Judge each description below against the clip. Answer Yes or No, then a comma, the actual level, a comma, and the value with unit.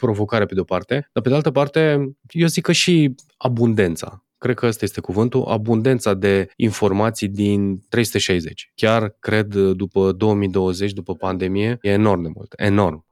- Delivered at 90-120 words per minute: No, average, 165 wpm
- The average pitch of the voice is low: Yes, low, 105 Hz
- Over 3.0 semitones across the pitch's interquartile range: Yes, average, 4.2 semitones